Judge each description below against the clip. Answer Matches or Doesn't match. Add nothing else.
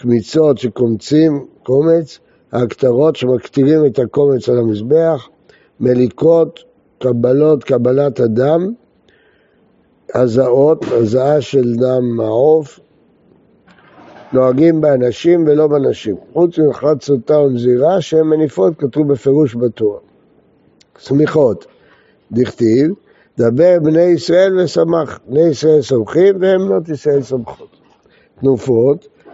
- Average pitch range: Matches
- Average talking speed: Doesn't match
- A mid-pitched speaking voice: Matches